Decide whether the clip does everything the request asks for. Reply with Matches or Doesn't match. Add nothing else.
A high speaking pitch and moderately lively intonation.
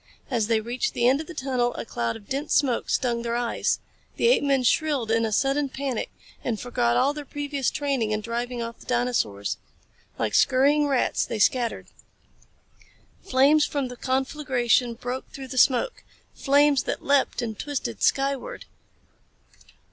Matches